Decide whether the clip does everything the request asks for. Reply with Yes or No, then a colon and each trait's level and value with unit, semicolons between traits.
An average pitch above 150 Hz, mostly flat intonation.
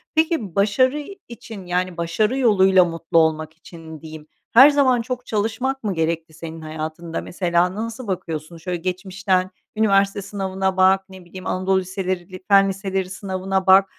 No: high, 190 Hz; average, 3.1 semitones